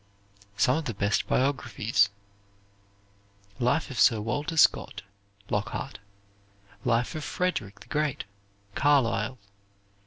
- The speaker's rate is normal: No, slow, 100 wpm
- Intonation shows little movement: No, average, 5.0 semitones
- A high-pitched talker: No, low, 125 Hz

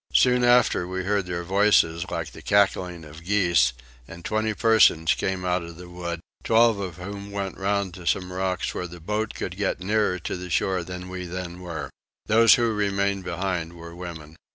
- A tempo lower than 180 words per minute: No, average, 190 wpm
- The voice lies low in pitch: Yes, very low, 90 Hz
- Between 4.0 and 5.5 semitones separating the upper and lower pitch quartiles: No, average, 2.7 semitones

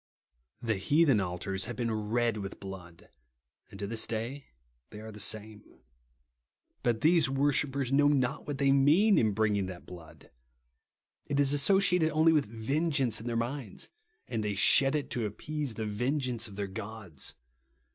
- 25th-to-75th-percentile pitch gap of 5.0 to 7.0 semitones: Yes, average, 5.3 semitones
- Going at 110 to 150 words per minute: No, average, 165 wpm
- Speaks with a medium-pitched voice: No, low, 115 Hz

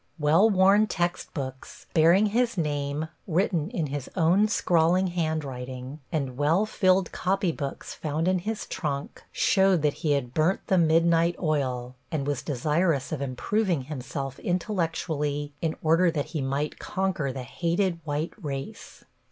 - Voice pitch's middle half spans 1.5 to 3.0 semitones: No, average, 4.2 semitones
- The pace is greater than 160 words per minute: No, average, 140 wpm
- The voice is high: No, medium, 160 Hz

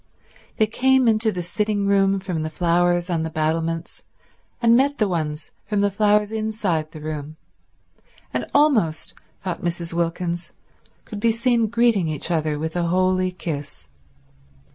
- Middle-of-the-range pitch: Yes, medium, 180 Hz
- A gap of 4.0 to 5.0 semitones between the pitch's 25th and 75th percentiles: Yes, average, 4.7 semitones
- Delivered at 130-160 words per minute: Yes, average, 150 wpm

